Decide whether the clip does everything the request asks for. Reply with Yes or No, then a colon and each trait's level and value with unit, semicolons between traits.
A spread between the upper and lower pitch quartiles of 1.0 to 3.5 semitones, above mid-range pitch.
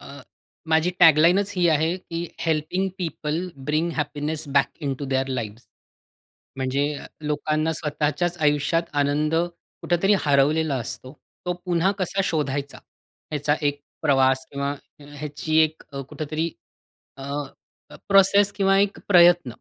No: average, 3.2 semitones; medium, 155 Hz